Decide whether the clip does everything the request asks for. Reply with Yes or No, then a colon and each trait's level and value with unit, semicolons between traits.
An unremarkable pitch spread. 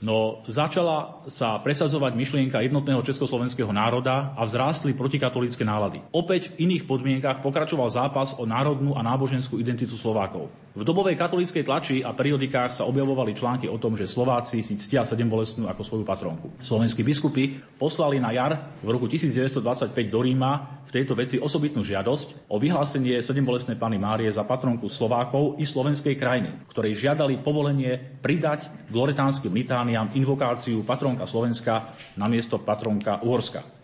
Yes: average, 3.3 semitones